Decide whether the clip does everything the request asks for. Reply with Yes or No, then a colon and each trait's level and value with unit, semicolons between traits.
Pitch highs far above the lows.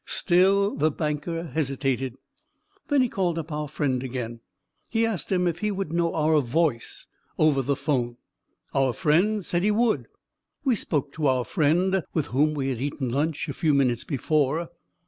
No: average, 4.4 semitones